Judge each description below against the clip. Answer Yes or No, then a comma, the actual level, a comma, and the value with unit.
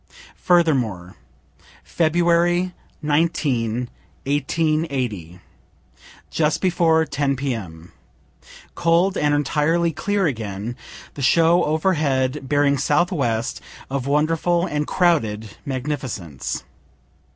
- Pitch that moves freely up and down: No, average, 5.0 semitones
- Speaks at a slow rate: Yes, slow, 80 wpm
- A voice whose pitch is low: No, medium, 145 Hz